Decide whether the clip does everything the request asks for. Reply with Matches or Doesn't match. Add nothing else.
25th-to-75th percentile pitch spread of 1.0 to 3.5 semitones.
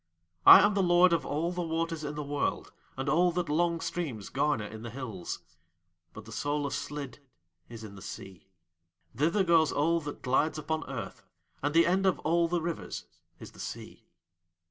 Doesn't match